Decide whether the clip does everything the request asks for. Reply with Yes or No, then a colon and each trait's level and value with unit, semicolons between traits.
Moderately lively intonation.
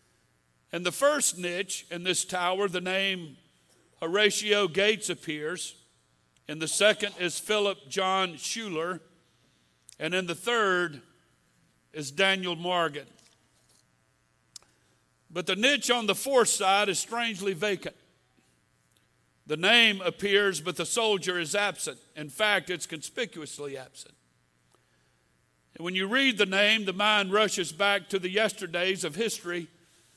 No: wide, 5.8 semitones